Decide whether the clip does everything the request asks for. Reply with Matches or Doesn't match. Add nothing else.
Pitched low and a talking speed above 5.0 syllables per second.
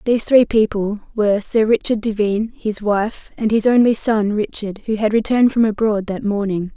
Doesn't match